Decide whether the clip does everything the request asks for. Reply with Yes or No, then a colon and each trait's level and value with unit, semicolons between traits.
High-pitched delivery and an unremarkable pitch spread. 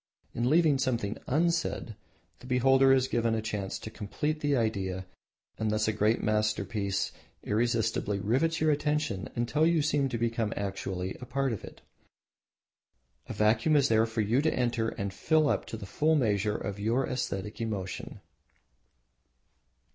No: low, 115 Hz; average, 4.5 semitones